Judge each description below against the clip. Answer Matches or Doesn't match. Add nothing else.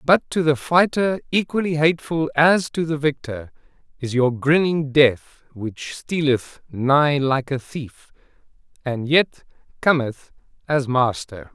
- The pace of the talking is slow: Matches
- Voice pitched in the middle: Matches